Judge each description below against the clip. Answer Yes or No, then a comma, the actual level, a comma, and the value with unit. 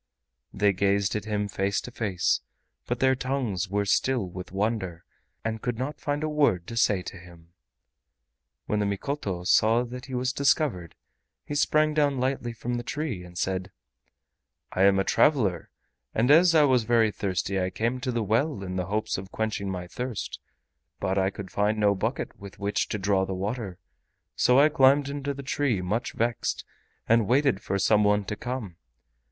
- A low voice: Yes, low, 110 Hz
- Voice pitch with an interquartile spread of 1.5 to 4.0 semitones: No, average, 5.0 semitones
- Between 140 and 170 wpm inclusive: No, average, 185 wpm